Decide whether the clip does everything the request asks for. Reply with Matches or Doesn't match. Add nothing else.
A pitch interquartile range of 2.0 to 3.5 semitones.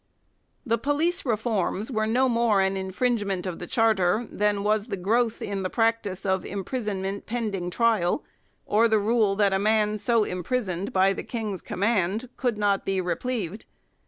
Matches